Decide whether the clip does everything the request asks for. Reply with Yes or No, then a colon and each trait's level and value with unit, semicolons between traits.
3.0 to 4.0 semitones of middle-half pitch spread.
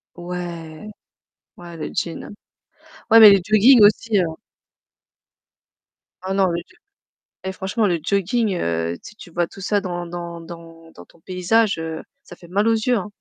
Yes: average, 3.6 semitones